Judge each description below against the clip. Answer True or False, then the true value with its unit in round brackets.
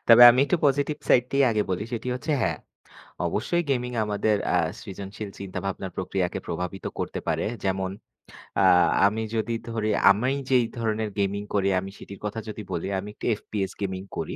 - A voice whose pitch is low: True (105 Hz)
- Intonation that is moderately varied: True (3.3 semitones)